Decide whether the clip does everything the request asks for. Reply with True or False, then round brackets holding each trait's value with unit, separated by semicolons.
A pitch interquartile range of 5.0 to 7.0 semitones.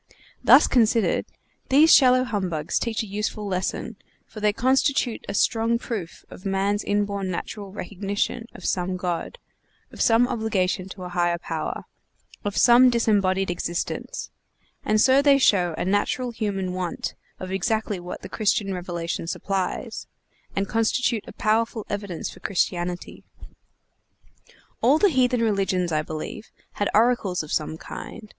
False (3.9 semitones)